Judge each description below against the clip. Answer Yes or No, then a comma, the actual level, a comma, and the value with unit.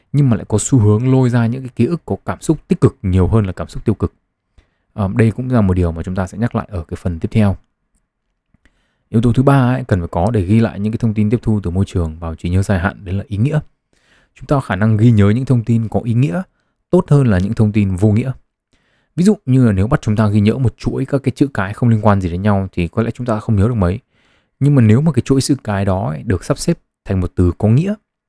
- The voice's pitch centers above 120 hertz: No, low, 110 Hz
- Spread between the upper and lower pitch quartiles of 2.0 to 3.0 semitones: No, average, 4.3 semitones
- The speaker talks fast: Yes, fast, 295 wpm